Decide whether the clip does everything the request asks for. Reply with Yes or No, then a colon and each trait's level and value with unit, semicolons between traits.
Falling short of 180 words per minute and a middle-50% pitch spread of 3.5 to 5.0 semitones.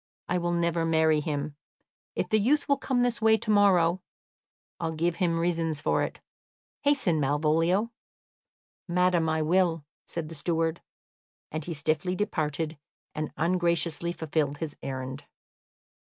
No: average, 140 wpm; narrow, 2.5 semitones